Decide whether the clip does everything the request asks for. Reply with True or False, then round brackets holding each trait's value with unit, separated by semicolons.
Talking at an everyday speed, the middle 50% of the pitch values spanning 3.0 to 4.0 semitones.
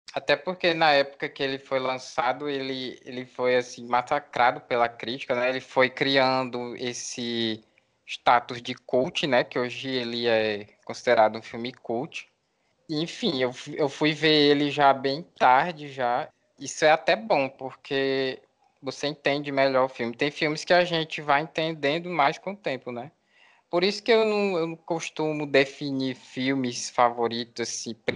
True (165 wpm; 3.6 semitones)